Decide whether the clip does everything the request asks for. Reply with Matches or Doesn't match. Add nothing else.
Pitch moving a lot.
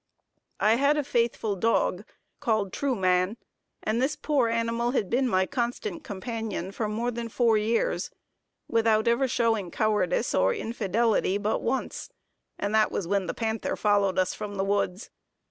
Doesn't match